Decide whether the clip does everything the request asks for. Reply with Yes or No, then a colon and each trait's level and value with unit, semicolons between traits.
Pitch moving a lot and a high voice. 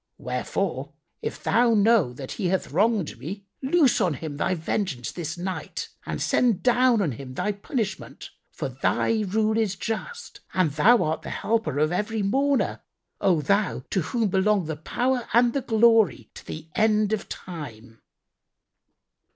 Yes: wide, 6.2 semitones; high, 200 Hz